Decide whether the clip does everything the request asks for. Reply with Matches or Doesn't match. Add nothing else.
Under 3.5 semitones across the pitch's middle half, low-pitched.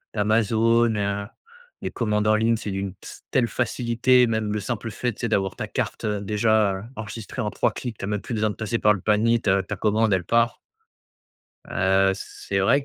Matches